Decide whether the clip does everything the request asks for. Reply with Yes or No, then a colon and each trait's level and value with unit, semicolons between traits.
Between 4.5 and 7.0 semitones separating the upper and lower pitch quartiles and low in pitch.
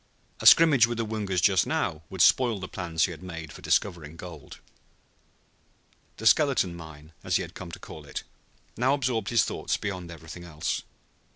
Yes: average, 5.3 semitones; very low, 90 Hz